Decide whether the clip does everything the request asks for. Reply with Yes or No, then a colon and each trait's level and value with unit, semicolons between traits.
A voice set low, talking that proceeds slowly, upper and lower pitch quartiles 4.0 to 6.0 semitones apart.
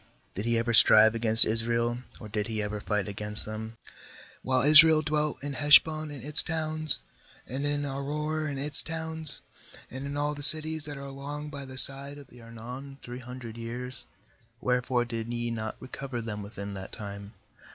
No: low, 130 Hz; average, 185 wpm; average, 4.3 semitones